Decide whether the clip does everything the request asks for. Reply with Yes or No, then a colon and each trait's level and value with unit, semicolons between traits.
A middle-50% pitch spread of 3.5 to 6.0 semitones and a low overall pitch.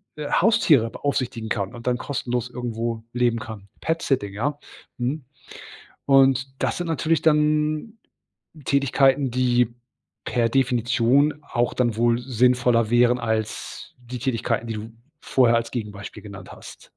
No: average, 2.8 semitones; low, 125 Hz